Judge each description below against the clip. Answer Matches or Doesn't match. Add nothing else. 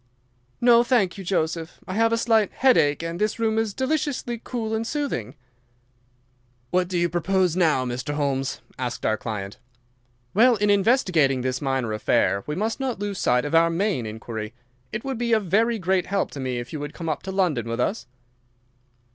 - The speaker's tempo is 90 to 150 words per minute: Doesn't match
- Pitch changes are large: Matches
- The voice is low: Doesn't match